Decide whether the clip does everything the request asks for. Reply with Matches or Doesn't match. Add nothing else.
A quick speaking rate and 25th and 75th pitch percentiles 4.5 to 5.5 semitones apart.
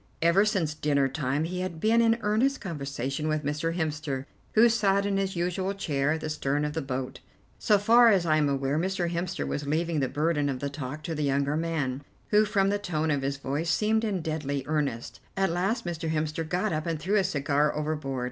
Matches